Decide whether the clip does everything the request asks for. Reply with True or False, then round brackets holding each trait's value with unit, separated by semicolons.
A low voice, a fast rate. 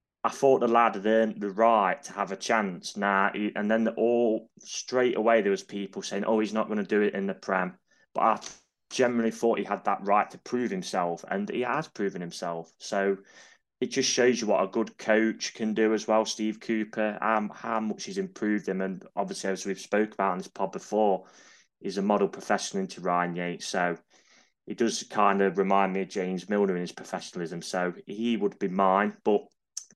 True (105 Hz; 210 wpm)